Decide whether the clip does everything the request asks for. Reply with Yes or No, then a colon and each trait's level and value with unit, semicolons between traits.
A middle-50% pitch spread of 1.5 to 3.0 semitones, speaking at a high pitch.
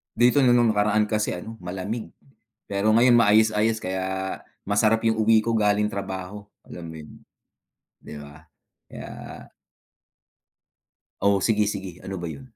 No: average, 2.7 semitones; low, 105 Hz